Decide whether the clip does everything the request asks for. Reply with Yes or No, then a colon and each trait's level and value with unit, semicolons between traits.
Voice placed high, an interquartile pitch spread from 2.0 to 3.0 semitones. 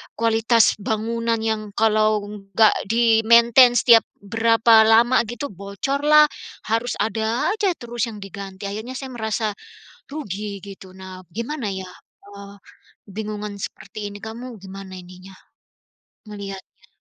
Yes: high, 220 Hz; average, 2.7 semitones